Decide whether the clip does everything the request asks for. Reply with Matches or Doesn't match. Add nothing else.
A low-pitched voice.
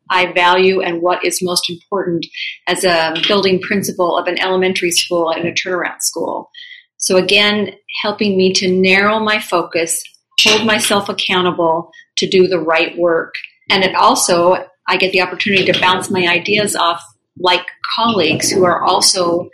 Doesn't match